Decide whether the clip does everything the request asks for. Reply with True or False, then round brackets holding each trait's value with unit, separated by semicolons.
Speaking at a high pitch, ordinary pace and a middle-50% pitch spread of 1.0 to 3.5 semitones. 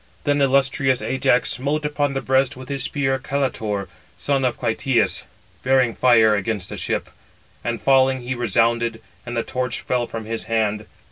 False (125 Hz; 160 wpm; 2.8 semitones)